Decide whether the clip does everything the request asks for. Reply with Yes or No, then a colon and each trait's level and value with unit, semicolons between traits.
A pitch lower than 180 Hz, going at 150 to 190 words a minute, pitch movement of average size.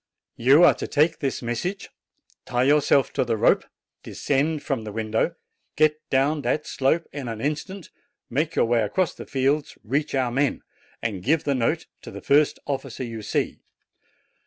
Yes: medium, 140 Hz; average, 170 wpm; average, 4.2 semitones